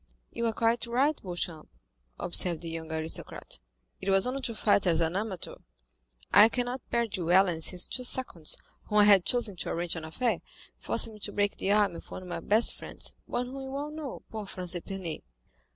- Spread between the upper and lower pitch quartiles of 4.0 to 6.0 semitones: Yes, average, 5.2 semitones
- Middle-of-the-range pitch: No, high, 205 Hz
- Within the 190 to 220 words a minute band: Yes, average, 200 wpm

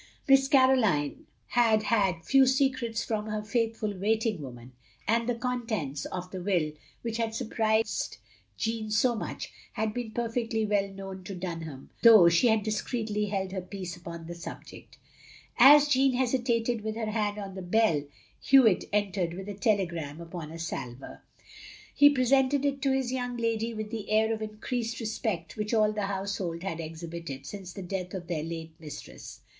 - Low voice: No, high, 215 Hz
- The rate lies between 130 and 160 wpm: No, average, 170 wpm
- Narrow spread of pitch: No, average, 4.4 semitones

